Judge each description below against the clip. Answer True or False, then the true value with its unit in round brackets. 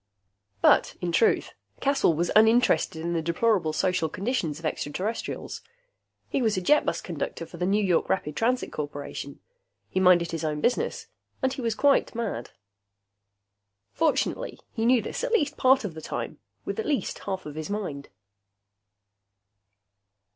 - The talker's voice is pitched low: False (185 Hz)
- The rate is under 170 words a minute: True (155 wpm)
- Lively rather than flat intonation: True (6.8 semitones)